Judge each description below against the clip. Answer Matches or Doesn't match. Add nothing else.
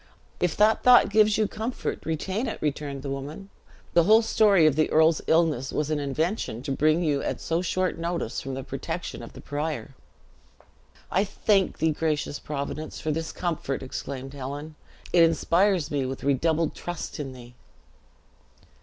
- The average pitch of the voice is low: Doesn't match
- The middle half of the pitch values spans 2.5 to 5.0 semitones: Matches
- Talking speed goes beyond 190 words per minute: Doesn't match